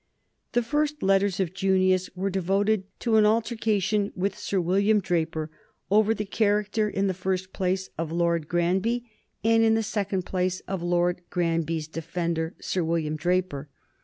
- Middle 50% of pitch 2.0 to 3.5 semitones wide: Yes, average, 3.2 semitones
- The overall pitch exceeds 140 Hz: Yes, high, 190 Hz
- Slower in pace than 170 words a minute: Yes, average, 160 wpm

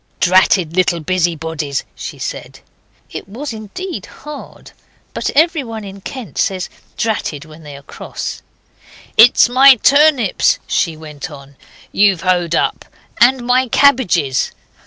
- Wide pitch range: Yes, wide, 7.7 semitones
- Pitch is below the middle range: No, high, 195 Hz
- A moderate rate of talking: No, slow, 125 wpm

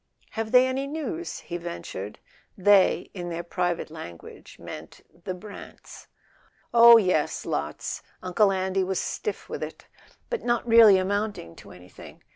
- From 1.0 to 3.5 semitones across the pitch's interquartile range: No, average, 5.0 semitones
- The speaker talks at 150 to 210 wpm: No, average, 140 wpm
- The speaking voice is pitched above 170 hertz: Yes, high, 190 Hz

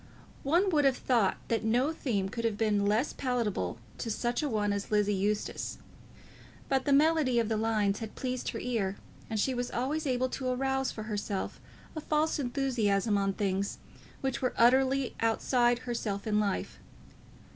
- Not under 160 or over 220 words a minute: Yes, average, 170 wpm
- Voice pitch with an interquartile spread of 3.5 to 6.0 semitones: Yes, average, 4.2 semitones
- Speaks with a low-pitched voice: No, high, 235 Hz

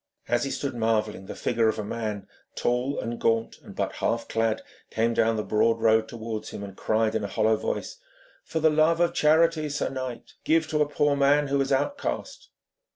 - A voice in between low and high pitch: No, low, 120 Hz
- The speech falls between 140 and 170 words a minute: No, fast, 205 wpm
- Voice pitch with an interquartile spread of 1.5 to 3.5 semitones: No, average, 4.8 semitones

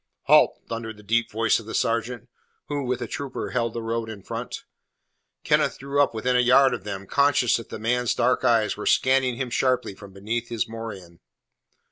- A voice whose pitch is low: Yes, low, 115 Hz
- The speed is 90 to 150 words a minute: No, average, 195 wpm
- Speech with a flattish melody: Yes, narrow, 2.2 semitones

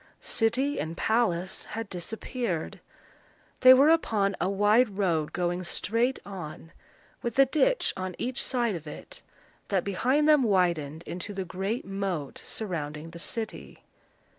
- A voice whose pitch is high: Yes, high, 200 Hz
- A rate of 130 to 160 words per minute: Yes, average, 140 wpm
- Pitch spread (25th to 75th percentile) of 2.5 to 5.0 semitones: No, wide, 5.5 semitones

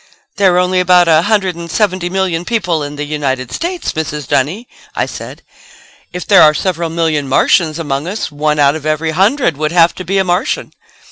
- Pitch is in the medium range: Yes, medium, 170 Hz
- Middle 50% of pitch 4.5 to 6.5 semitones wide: No, average, 3.4 semitones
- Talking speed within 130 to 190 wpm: No, average, 200 wpm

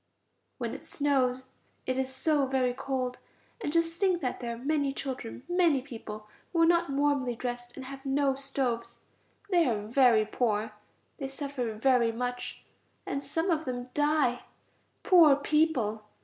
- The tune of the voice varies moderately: Yes, average, 3.0 semitones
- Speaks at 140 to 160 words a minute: Yes, average, 155 wpm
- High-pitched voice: Yes, very high, 265 Hz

